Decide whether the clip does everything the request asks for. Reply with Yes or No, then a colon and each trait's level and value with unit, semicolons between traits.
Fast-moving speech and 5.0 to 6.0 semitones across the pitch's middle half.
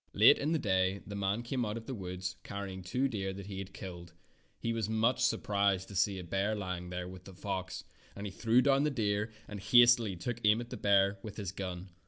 No: fast, 235 wpm; average, 3.2 semitones